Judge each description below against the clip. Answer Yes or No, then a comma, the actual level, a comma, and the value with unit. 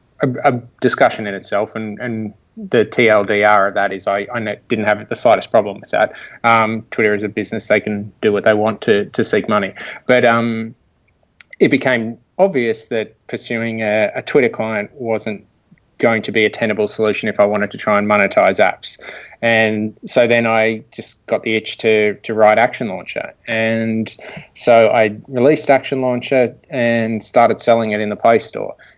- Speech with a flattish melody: Yes, narrow, 2.0 semitones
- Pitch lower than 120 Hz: Yes, low, 110 Hz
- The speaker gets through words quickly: No, average, 180 wpm